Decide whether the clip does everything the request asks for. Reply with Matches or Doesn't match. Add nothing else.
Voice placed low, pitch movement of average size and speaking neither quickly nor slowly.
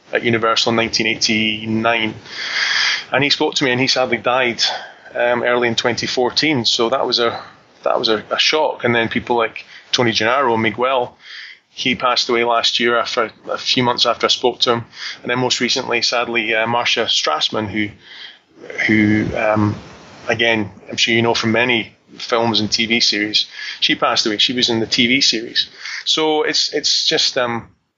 Doesn't match